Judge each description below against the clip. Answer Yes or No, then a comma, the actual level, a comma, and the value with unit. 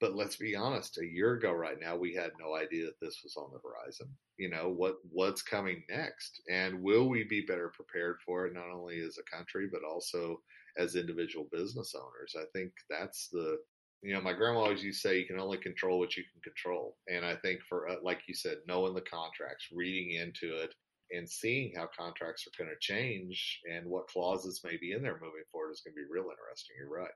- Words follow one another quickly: Yes, fast, 230 wpm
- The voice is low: Yes, very low, 95 Hz